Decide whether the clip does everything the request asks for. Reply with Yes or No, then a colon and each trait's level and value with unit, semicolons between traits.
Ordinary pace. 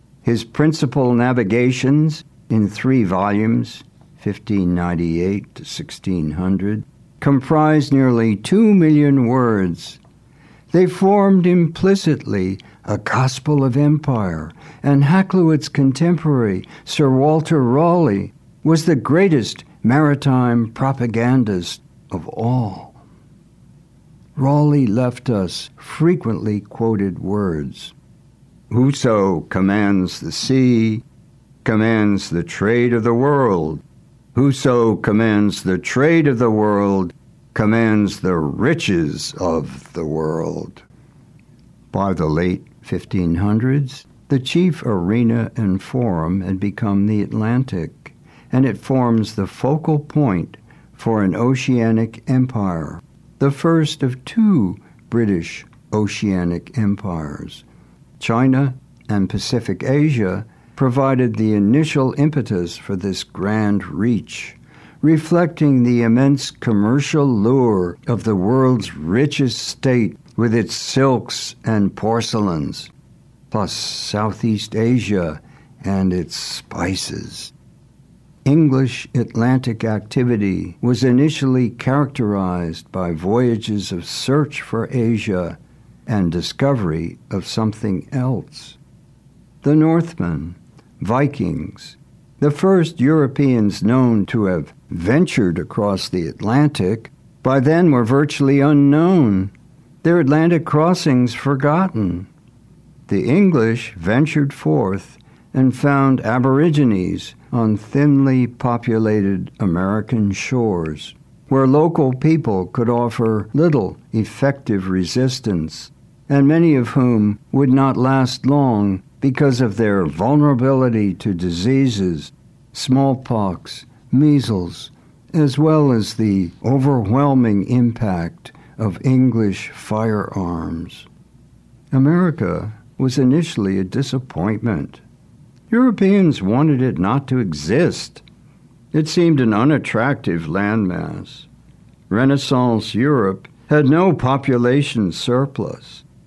No: slow, 95 wpm